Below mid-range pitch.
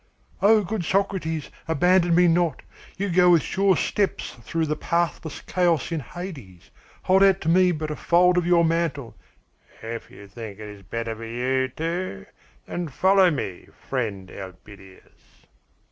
No: medium, 165 Hz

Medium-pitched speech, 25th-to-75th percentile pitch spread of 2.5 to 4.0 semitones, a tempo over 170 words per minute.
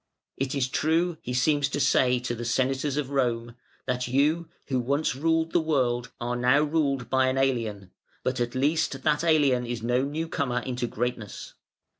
No: low, 130 Hz; average, 3.3 semitones; average, 180 wpm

